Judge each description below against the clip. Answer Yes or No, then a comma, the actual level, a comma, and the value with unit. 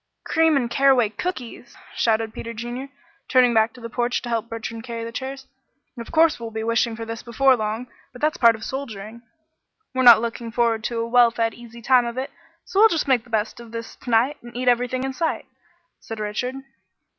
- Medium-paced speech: No, fast, 215 wpm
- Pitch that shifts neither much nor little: No, narrow, 2.1 semitones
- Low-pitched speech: No, high, 235 Hz